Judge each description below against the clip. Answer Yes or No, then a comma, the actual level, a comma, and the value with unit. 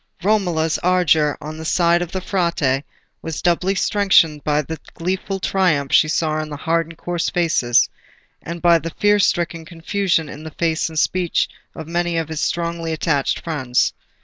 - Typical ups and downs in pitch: No, narrow, 2.1 semitones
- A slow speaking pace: No, average, 170 wpm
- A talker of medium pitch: Yes, medium, 165 Hz